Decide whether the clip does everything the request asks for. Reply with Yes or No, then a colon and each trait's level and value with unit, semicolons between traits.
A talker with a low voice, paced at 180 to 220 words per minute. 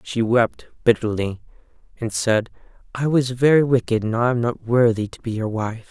Yes: low, 120 Hz; average, 185 wpm